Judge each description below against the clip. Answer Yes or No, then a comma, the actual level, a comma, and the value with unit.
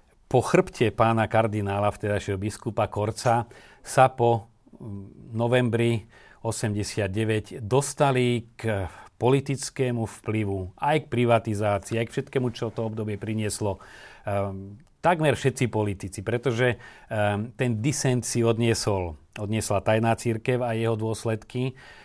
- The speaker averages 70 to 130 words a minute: Yes, slow, 110 wpm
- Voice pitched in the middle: No, low, 115 Hz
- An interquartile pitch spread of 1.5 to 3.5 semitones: Yes, average, 2.9 semitones